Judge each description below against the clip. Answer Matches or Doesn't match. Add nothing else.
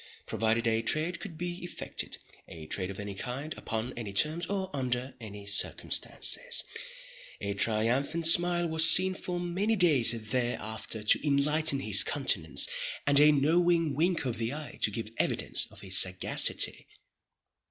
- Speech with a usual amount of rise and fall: Doesn't match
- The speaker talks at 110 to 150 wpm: Matches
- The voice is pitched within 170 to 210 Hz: Doesn't match